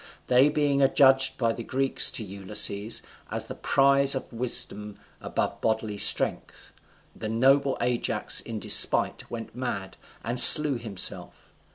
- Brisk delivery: No, slow, 135 wpm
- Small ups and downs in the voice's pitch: No, average, 3.9 semitones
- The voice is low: Yes, low, 120 Hz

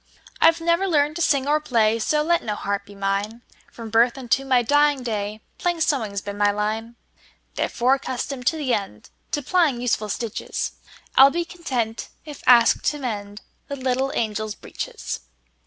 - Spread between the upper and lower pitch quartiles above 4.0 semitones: Yes, average, 5.3 semitones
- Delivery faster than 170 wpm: No, average, 155 wpm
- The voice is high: Yes, high, 245 Hz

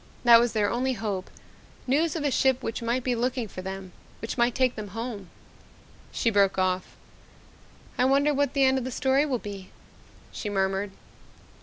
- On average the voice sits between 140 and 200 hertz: No, high, 235 Hz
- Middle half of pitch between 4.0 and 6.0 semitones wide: Yes, average, 4.5 semitones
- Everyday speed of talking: Yes, average, 185 wpm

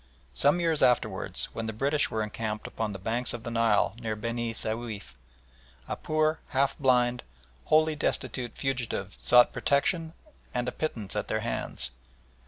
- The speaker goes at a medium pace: Yes, average, 155 wpm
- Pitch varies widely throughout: No, average, 4.1 semitones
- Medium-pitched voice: No, low, 120 Hz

